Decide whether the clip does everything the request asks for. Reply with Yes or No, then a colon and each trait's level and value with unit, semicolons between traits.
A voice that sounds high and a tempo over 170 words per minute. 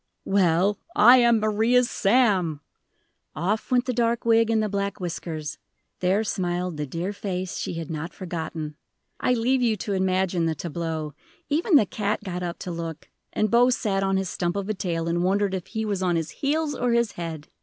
Yes: high, 195 Hz; average, 195 wpm